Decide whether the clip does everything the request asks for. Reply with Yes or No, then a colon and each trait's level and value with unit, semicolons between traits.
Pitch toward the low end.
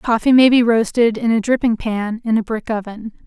No: high, 225 Hz